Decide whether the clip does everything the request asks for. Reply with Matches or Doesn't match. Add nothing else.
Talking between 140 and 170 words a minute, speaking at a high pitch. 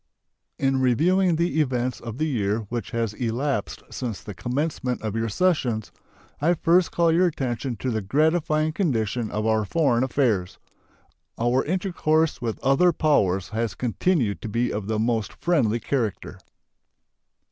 Doesn't match